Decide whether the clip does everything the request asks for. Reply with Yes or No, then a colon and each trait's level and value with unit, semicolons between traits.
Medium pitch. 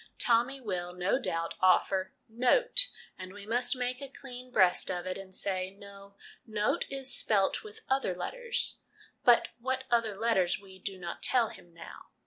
No: high, 215 Hz